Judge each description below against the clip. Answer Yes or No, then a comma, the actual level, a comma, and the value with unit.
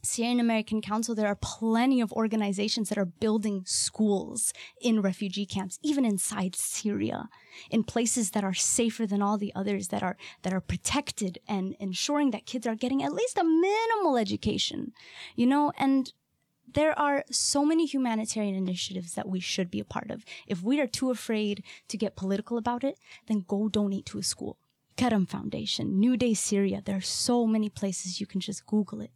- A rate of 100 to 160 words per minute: No, average, 185 wpm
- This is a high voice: Yes, high, 215 Hz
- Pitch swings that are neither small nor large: Yes, average, 3.6 semitones